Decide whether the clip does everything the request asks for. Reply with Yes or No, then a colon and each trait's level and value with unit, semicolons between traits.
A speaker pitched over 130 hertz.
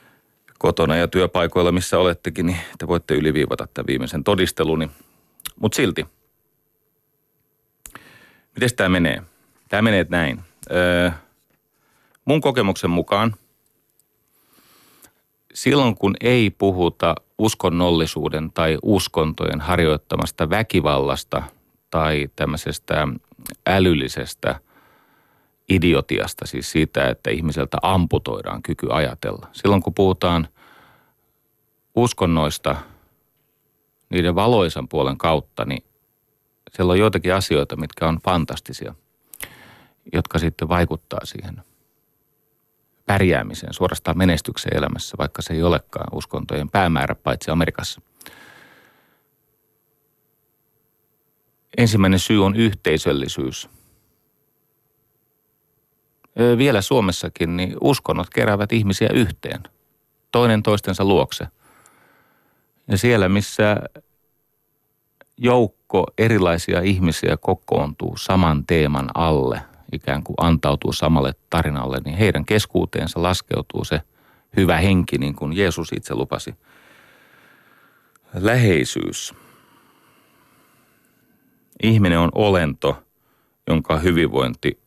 No: very low, 90 Hz